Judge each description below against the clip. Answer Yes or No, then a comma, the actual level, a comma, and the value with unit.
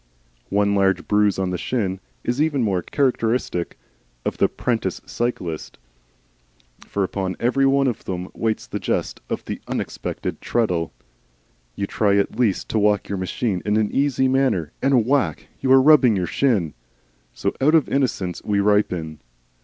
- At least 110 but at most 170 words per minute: Yes, average, 160 wpm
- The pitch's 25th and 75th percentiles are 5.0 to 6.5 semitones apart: Yes, wide, 5.6 semitones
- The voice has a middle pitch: No, low, 105 Hz